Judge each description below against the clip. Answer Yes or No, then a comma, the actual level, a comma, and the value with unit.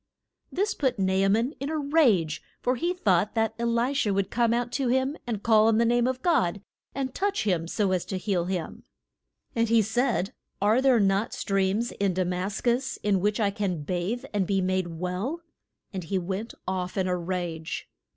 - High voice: Yes, high, 205 Hz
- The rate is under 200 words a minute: No, fast, 205 wpm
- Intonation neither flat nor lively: Yes, average, 4.5 semitones